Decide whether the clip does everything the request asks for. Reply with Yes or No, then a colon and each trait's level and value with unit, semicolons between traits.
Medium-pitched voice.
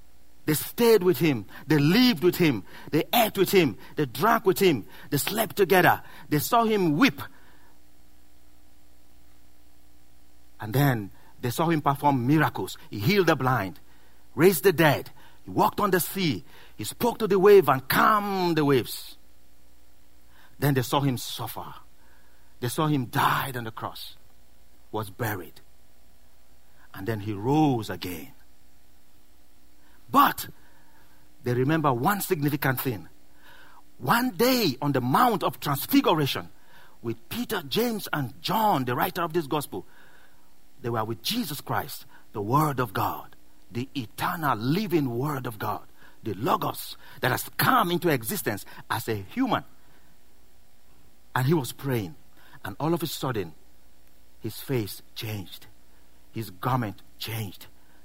No: low, 120 Hz